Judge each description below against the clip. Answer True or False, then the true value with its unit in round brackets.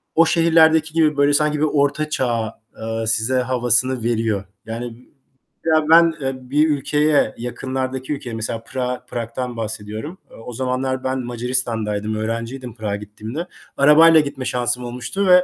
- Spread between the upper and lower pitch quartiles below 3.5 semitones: False (4.5 semitones)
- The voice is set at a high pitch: False (130 Hz)